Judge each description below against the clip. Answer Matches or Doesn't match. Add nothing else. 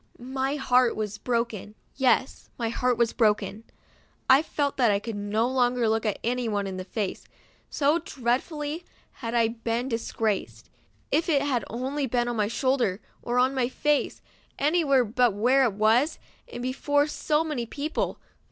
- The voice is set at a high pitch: Matches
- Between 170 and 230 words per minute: Doesn't match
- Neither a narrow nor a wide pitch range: Matches